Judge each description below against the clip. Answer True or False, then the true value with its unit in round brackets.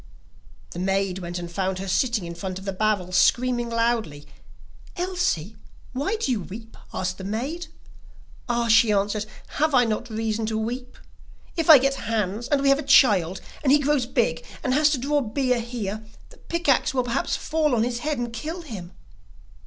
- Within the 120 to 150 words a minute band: False (190 wpm)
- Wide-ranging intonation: True (5.7 semitones)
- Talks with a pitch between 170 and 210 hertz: False (230 Hz)